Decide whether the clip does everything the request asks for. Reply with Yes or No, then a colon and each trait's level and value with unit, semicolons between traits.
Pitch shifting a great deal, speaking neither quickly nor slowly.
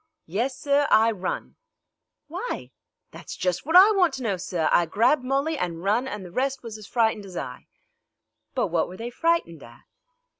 Yes: wide, 7.3 semitones; average, 185 wpm